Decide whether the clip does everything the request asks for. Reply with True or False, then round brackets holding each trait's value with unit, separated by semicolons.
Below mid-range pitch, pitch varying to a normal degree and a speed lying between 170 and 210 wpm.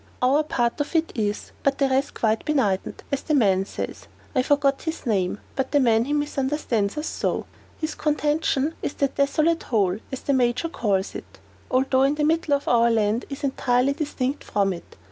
False (270 Hz; 4.3 semitones; 190 wpm)